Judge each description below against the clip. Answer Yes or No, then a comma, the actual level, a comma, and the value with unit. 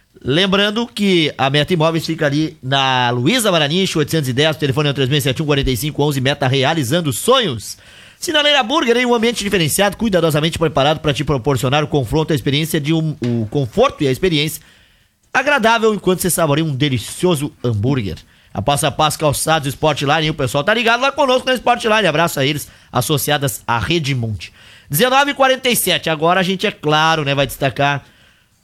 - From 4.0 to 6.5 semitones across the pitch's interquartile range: Yes, average, 5.0 semitones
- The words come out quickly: No, average, 165 wpm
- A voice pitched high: No, medium, 150 Hz